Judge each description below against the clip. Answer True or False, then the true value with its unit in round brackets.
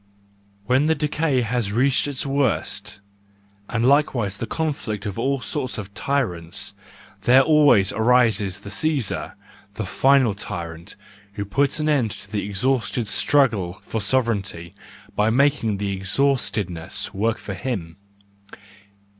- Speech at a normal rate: False (130 wpm)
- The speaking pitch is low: True (115 Hz)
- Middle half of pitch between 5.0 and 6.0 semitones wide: True (5.4 semitones)